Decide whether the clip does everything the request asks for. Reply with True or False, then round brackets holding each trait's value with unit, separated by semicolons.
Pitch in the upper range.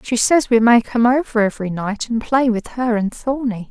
True (235 Hz)